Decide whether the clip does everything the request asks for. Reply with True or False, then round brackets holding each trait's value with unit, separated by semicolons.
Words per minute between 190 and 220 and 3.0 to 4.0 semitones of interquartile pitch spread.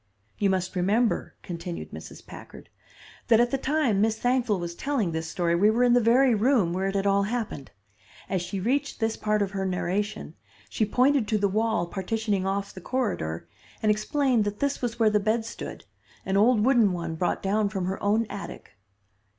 True (195 wpm; 3.6 semitones)